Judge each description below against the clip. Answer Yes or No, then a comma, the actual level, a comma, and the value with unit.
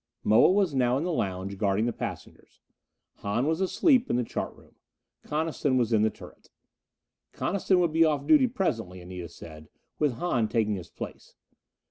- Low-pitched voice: Yes, low, 125 Hz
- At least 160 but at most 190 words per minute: Yes, average, 170 wpm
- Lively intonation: Yes, wide, 8.2 semitones